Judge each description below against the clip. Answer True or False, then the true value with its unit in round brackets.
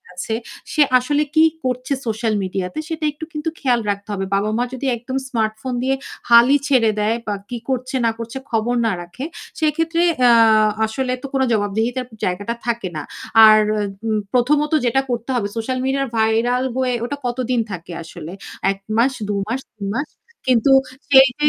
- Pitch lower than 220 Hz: False (245 Hz)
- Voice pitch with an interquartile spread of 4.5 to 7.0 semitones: False (3.5 semitones)